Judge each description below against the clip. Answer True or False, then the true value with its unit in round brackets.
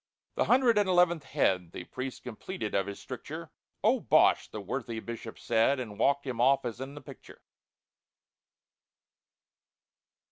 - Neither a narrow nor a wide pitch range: True (4.4 semitones)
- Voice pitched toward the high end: False (130 Hz)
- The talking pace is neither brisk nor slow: True (145 wpm)